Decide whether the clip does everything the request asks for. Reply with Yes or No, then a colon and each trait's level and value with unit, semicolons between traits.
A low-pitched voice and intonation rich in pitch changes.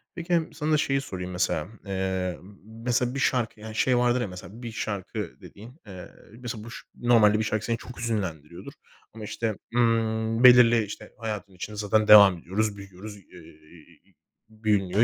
No: low, 110 Hz; average, 3.4 semitones